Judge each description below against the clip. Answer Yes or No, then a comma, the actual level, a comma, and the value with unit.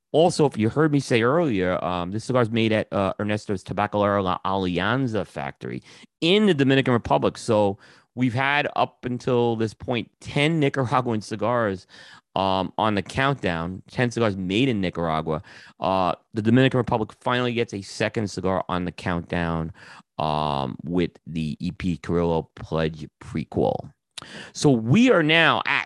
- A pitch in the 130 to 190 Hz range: No, low, 105 Hz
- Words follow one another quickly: No, average, 155 wpm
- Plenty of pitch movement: Yes, wide, 5.8 semitones